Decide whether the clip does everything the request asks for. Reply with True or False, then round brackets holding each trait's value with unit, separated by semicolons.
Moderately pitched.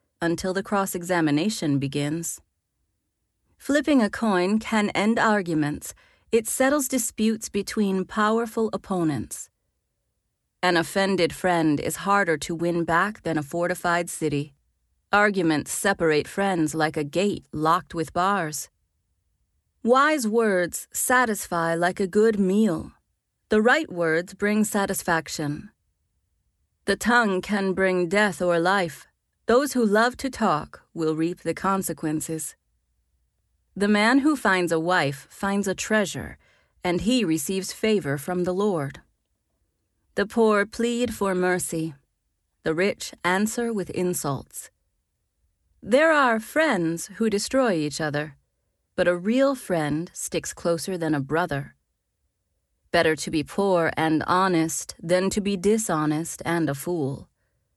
True (180 Hz)